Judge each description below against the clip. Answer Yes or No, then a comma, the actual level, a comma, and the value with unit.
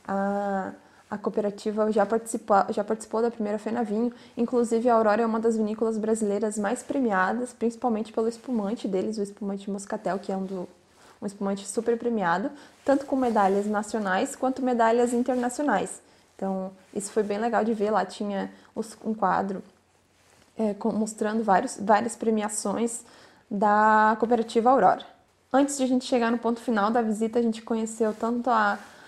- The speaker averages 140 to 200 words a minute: Yes, average, 160 wpm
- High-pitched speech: Yes, high, 220 Hz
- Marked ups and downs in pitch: No, average, 2.7 semitones